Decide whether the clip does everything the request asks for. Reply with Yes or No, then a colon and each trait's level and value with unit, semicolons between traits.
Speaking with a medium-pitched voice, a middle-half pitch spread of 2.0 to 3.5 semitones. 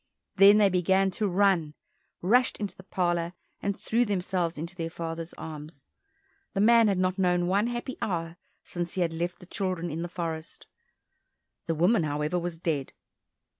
Yes: medium, 180 Hz; average, 2.9 semitones